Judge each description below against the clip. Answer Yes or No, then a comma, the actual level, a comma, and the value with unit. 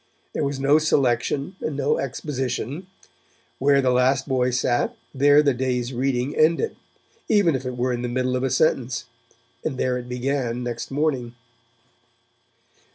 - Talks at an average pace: Yes, average, 155 wpm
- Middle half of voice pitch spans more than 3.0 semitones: No, narrow, 2.4 semitones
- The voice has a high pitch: No, low, 130 Hz